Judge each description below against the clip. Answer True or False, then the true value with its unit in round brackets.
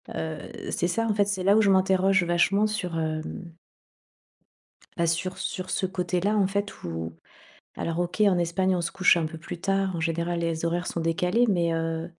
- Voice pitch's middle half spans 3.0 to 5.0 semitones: False (2.5 semitones)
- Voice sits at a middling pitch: True (175 Hz)